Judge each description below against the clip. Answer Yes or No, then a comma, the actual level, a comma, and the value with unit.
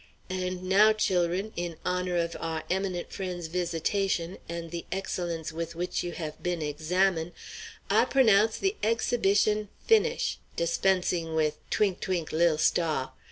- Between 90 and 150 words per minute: Yes, average, 140 wpm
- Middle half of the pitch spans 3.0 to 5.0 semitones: No, narrow, 2.6 semitones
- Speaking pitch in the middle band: Yes, medium, 180 Hz